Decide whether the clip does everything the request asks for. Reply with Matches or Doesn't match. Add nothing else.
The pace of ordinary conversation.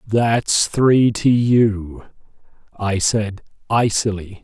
Doesn't match